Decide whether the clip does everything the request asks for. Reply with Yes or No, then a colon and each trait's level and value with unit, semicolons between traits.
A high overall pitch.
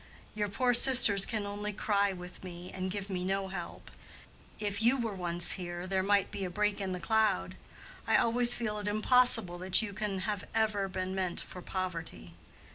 Yes: high, 195 Hz